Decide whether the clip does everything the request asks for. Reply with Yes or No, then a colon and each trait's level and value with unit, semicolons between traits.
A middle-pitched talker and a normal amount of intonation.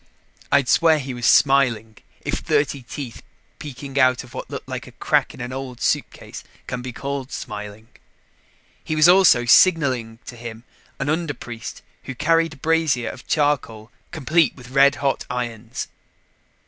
No: low, 130 Hz; average, 3.4 semitones